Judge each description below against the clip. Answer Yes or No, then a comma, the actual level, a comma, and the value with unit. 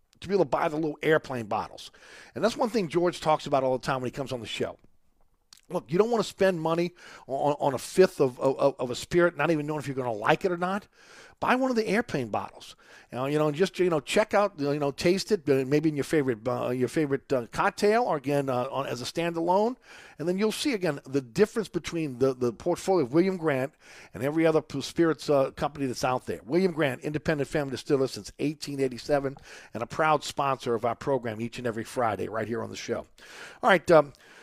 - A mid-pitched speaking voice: Yes, medium, 150 Hz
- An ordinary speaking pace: No, fast, 240 wpm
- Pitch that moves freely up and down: No, average, 4.8 semitones